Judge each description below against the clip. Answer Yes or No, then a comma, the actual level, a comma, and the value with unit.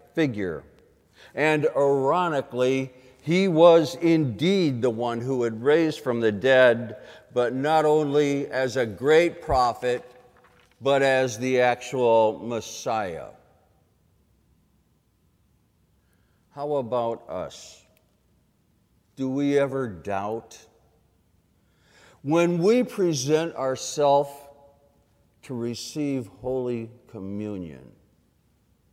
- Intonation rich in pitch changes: No, average, 3.8 semitones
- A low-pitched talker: Yes, low, 130 Hz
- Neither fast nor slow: No, slow, 85 wpm